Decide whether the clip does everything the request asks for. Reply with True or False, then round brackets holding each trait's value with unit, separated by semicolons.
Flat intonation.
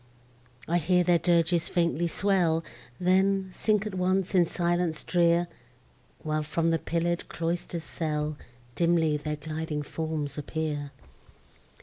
True (2.1 semitones)